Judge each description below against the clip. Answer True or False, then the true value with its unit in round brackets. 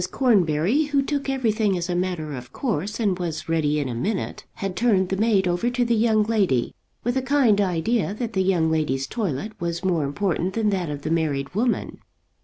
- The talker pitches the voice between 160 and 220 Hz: True (190 Hz)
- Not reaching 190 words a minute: False (205 wpm)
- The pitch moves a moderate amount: False (5.9 semitones)